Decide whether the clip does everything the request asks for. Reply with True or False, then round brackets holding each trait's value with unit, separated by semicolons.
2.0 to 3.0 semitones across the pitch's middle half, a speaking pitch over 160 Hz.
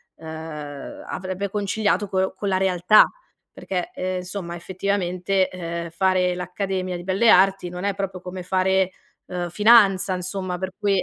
False (1.5 semitones; 185 Hz)